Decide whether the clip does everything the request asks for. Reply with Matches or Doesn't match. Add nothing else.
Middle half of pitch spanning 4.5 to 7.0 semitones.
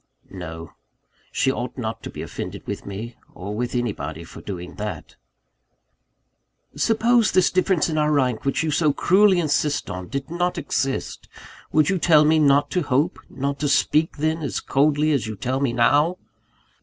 Matches